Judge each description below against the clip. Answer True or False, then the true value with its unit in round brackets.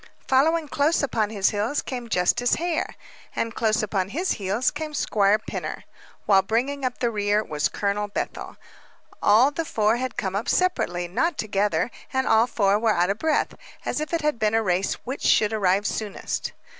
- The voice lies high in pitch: True (220 Hz)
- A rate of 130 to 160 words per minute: False (180 wpm)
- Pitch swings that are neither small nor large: True (4.7 semitones)